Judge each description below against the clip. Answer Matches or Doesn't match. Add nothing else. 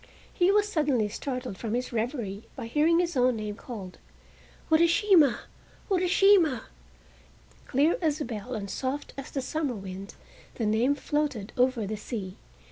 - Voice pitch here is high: Matches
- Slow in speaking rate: Doesn't match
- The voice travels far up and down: Matches